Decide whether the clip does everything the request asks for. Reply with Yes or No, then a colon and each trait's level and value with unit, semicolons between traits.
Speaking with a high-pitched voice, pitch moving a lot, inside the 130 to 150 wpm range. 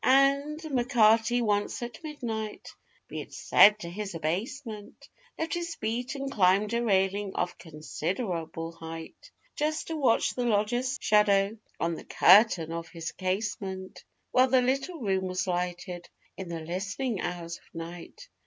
Yes: high, 210 Hz; wide, 5.9 semitones; average, 145 wpm